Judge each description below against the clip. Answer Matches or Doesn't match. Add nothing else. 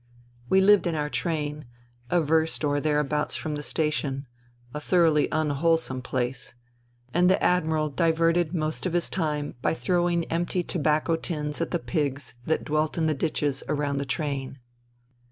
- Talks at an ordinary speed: Matches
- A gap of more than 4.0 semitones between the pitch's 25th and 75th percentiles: Doesn't match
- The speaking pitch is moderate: Matches